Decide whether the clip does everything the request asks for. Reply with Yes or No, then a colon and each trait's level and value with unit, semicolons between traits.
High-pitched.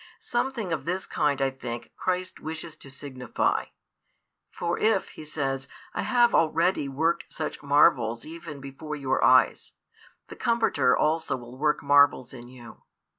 No: medium, 150 Hz